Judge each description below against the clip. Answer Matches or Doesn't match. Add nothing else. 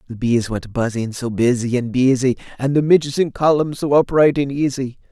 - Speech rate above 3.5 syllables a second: Matches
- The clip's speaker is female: Doesn't match